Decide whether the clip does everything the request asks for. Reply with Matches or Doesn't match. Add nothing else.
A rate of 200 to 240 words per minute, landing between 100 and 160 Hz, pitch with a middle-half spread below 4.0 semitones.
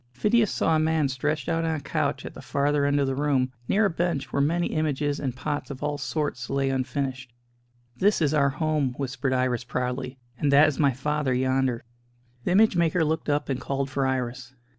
Matches